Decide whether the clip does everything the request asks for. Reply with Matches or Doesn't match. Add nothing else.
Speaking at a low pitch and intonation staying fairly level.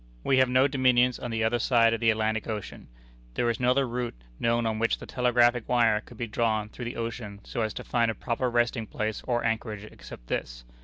Matches